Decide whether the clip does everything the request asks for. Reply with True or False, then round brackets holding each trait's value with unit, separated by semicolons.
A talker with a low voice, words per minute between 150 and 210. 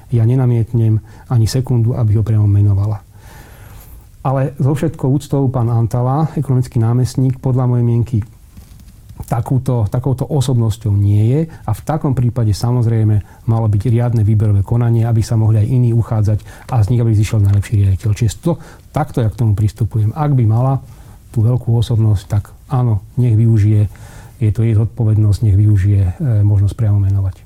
True (115 Hz; 160 wpm)